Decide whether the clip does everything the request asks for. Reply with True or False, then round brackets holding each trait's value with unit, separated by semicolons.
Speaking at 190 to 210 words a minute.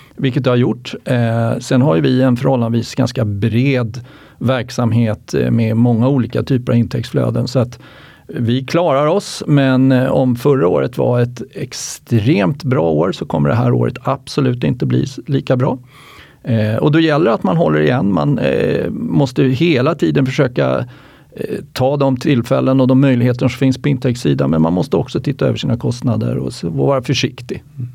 False (175 wpm)